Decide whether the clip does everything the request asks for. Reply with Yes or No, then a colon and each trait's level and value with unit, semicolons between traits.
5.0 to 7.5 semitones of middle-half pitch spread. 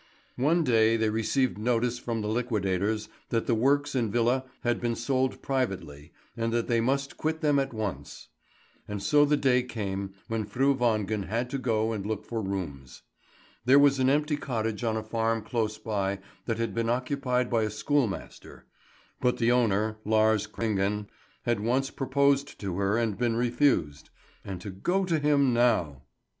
No: average, 3.5 semitones